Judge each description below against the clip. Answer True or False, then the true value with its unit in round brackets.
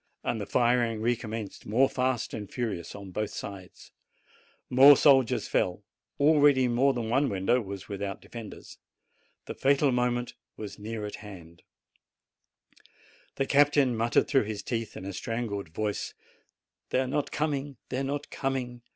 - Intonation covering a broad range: False (4.4 semitones)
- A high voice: False (120 Hz)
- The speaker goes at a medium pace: True (150 wpm)